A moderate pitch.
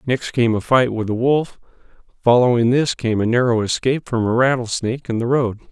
No: low, 120 Hz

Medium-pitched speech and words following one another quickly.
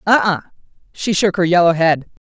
No: medium, 180 Hz; average, 185 wpm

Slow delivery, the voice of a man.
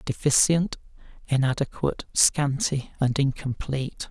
Yes: slow, 75 wpm; male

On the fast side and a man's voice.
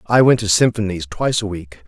Yes: fast, 225 wpm; male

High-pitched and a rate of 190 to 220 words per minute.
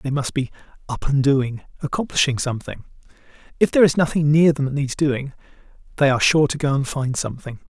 No: medium, 140 Hz; average, 195 wpm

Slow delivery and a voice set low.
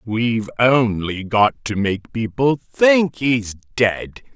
Yes: slow, 125 wpm; low, 115 Hz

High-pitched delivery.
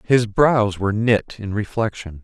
No: low, 105 Hz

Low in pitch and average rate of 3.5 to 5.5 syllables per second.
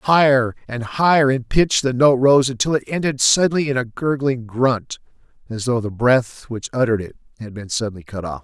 Yes: low, 125 Hz; 5.2 syllables/s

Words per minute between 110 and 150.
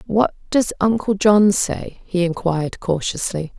Yes: slow, 135 wpm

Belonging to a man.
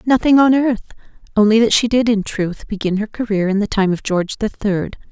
No: female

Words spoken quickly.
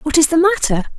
Yes: fast, 245 wpm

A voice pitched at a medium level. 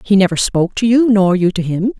No: high, 200 Hz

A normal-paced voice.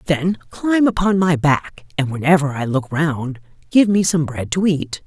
Yes: average, 190 wpm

